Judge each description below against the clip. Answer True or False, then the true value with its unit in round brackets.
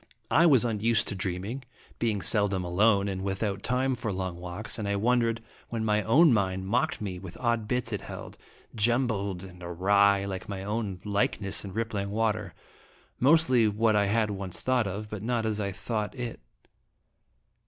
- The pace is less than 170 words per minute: False (175 wpm)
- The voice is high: False (105 Hz)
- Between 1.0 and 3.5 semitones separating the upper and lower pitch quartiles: True (2.9 semitones)